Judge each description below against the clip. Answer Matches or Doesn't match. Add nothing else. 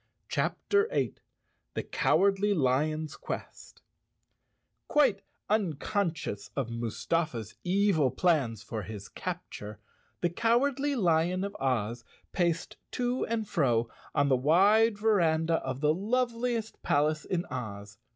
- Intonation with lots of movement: Matches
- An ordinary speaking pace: Doesn't match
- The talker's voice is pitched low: Doesn't match